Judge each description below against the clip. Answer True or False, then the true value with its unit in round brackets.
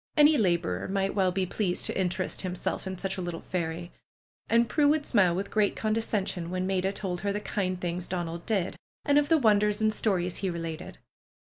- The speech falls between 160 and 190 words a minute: False (205 wpm)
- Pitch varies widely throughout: False (3.0 semitones)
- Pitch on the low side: False (190 Hz)